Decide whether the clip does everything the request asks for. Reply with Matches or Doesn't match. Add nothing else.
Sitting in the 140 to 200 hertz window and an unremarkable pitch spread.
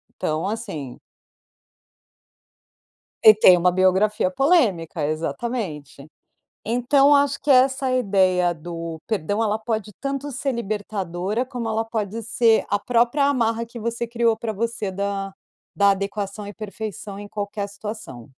Doesn't match